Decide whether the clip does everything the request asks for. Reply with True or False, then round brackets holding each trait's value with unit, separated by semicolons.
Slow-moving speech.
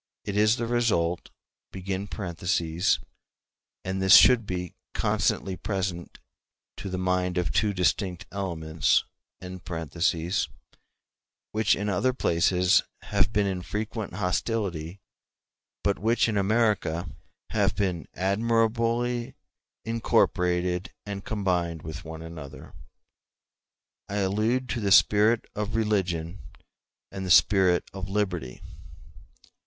True (105 wpm)